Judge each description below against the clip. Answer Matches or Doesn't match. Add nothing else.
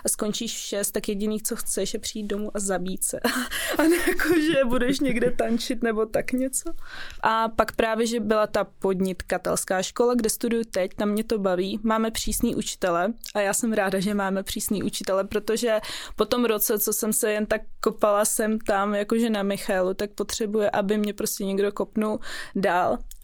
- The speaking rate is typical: Doesn't match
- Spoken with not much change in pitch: Matches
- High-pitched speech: Matches